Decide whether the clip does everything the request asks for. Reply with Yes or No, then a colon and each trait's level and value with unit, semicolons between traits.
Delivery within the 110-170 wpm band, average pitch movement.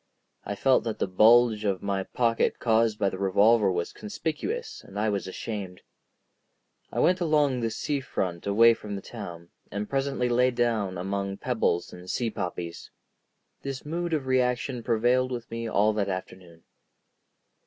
Yes: average, 160 wpm; average, 4.4 semitones